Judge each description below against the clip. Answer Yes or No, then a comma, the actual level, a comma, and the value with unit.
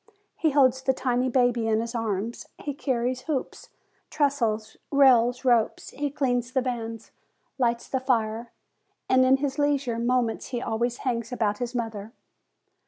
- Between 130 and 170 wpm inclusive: Yes, average, 150 wpm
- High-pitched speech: Yes, high, 245 Hz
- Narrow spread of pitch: Yes, narrow, 2.3 semitones